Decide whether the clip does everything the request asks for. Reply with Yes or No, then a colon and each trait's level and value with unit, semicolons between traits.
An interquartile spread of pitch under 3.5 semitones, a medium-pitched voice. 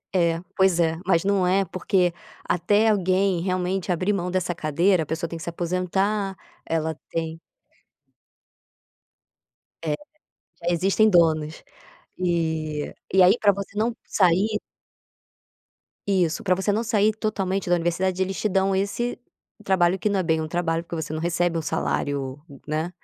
Yes: average, 2.7 semitones; medium, 180 Hz